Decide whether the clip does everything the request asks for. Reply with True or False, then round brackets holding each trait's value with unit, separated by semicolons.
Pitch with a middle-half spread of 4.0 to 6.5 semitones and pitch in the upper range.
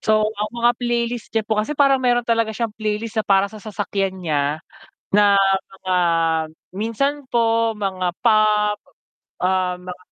False (2.8 semitones; 215 Hz)